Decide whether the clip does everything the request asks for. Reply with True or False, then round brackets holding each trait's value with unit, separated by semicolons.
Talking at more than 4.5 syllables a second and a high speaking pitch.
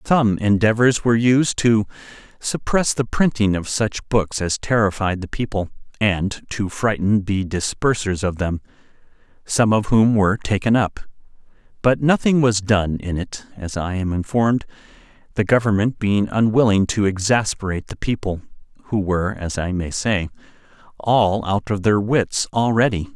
False (4.7 syllables/s; 105 Hz)